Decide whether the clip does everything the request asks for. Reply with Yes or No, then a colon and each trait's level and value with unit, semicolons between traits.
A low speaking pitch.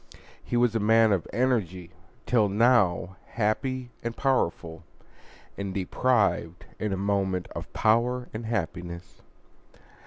Yes: low, 105 Hz